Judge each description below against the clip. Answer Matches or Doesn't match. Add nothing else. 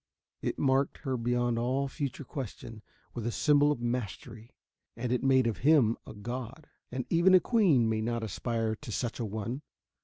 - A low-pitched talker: Matches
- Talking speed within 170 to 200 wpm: Matches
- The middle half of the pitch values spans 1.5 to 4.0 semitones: Matches